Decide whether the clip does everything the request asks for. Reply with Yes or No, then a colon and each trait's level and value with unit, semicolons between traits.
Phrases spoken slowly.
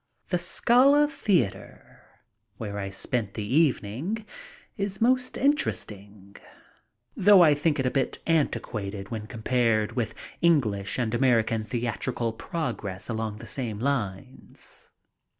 Yes: slow, 115 wpm